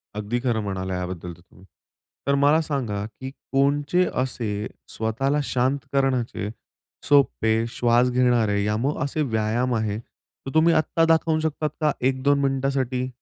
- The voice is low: Yes, low, 125 Hz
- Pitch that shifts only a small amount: No, average, 4.3 semitones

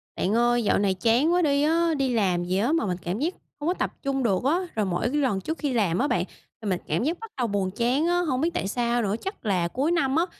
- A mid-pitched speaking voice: No, high, 245 Hz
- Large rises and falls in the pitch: Yes, wide, 7.3 semitones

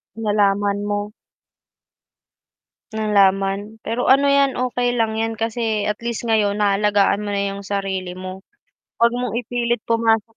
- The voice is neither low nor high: No, high, 210 Hz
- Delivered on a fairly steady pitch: Yes, narrow, 2.3 semitones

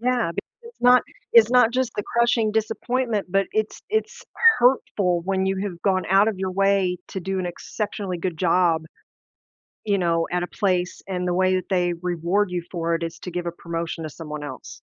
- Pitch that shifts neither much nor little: Yes, average, 3.6 semitones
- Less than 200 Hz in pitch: Yes, medium, 185 Hz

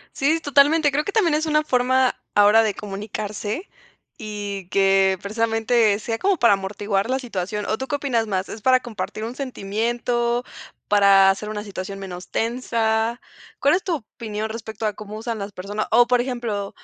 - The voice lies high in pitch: Yes, high, 220 Hz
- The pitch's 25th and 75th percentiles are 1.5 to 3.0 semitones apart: No, average, 3.6 semitones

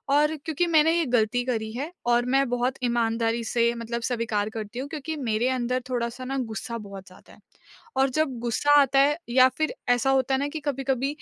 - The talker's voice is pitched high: Yes, very high, 250 Hz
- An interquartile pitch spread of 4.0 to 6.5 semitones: No, average, 2.8 semitones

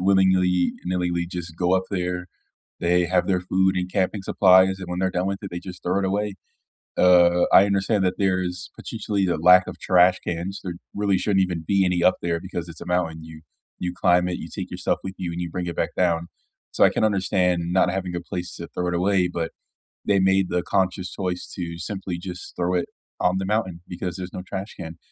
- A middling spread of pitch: No, narrow, 1.4 semitones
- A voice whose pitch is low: Yes, very low, 90 Hz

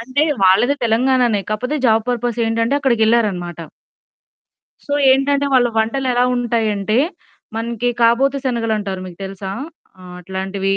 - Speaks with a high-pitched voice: Yes, high, 230 Hz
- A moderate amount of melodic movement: Yes, average, 3.6 semitones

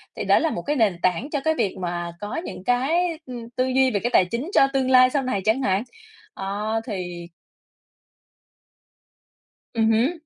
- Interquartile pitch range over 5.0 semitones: Yes, wide, 5.5 semitones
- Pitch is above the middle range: Yes, high, 235 Hz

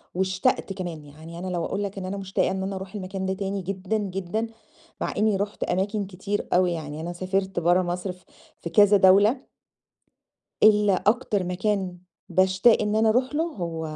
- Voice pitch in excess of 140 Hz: Yes, high, 190 Hz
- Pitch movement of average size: No, narrow, 2.2 semitones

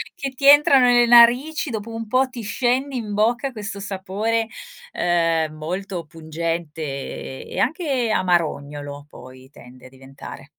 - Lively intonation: Yes, wide, 7.5 semitones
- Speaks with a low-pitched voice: No, high, 200 Hz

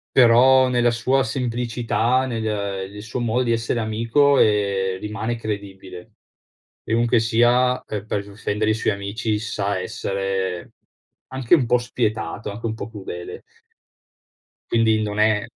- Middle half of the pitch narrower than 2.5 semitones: No, average, 2.8 semitones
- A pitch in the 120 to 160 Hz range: No, low, 110 Hz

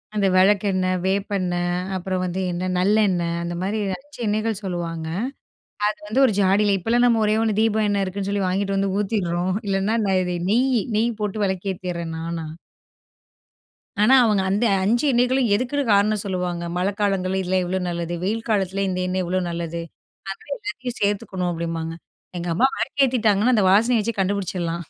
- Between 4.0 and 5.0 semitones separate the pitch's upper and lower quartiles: No, average, 2.9 semitones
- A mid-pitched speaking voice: No, high, 195 Hz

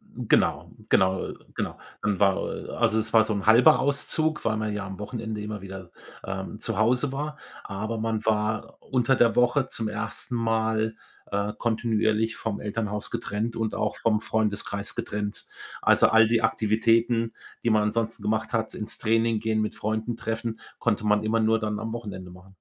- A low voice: Yes, low, 110 Hz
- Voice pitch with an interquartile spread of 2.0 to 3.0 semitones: No, narrow, 1.4 semitones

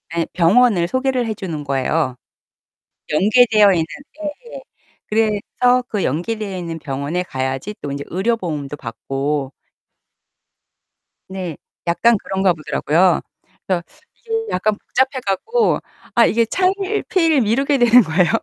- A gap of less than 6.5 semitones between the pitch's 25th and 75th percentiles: No, wide, 7.3 semitones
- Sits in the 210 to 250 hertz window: No, high, 195 Hz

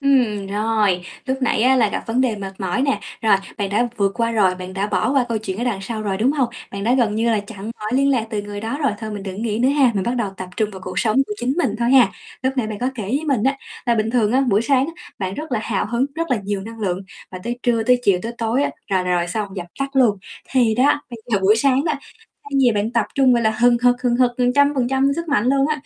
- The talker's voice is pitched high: Yes, high, 230 Hz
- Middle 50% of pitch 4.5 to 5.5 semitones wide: No, average, 4.0 semitones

